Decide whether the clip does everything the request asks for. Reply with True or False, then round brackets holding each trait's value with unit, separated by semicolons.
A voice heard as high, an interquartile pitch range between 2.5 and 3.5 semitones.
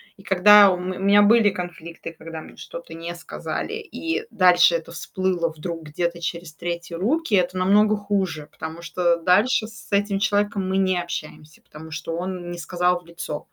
False (180 Hz; 2.9 semitones)